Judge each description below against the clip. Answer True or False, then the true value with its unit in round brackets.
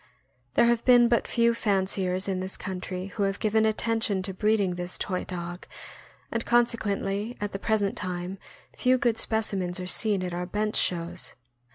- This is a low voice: False (200 Hz)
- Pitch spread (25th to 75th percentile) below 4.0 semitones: True (3.2 semitones)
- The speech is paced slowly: False (175 wpm)